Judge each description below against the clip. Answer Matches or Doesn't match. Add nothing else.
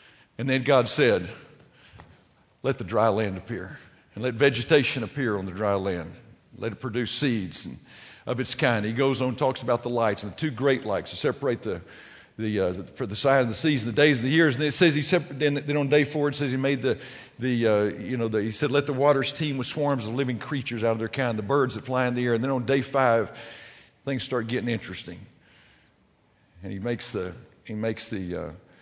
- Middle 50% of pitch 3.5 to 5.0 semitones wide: Matches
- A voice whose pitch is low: Matches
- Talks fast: Matches